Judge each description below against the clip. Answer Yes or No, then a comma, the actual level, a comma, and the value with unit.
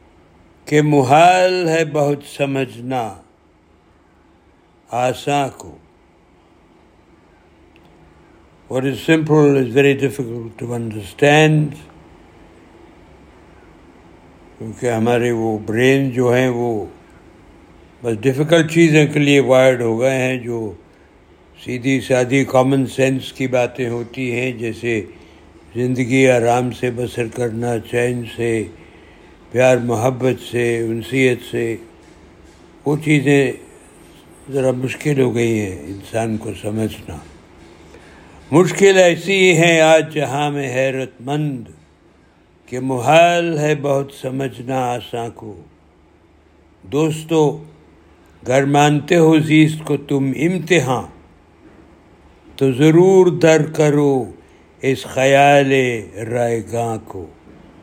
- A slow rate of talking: Yes, slow, 100 wpm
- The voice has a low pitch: Yes, low, 125 Hz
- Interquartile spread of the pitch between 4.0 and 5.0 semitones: Yes, average, 4.5 semitones